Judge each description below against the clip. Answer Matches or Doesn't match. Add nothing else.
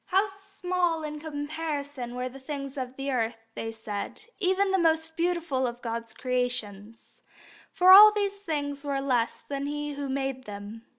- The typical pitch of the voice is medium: Doesn't match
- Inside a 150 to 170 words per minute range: Matches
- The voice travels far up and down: Doesn't match